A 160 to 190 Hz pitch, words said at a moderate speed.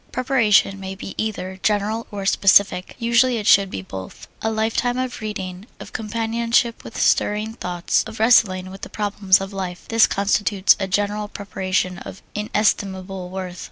No: high, 205 Hz; average, 160 wpm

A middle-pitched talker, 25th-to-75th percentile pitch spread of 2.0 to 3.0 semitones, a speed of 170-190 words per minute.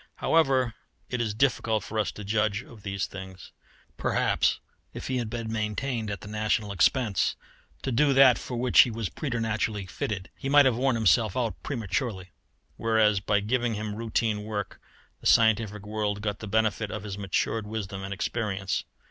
No: low, 110 Hz; narrow, 2.6 semitones; average, 175 wpm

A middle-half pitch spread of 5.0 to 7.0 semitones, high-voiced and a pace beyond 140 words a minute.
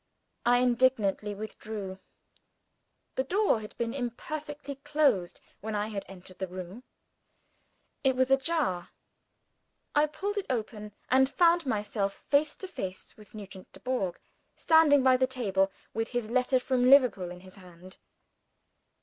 No: wide, 5.6 semitones; high, 240 Hz; slow, 135 wpm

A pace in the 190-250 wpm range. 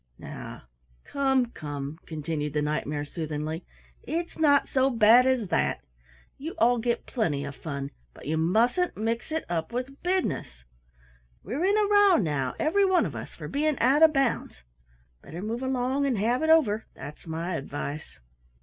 No: average, 170 wpm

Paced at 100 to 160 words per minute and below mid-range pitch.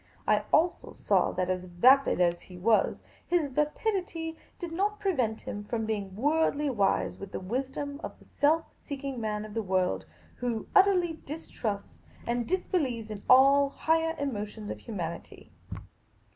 No: average, 150 wpm; very high, 255 Hz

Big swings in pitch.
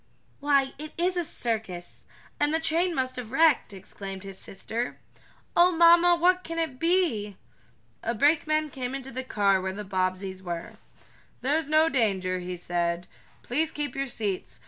Yes: wide, 8.6 semitones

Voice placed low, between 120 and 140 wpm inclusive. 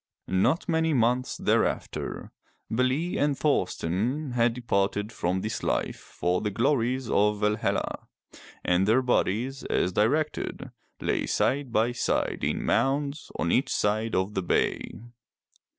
Yes: low, 115 Hz; slow, 135 wpm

